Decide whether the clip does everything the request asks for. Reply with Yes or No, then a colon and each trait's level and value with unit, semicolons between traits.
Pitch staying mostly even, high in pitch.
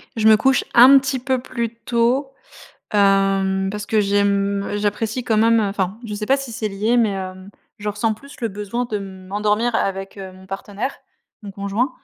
No: average, 3.0 semitones; high, 210 Hz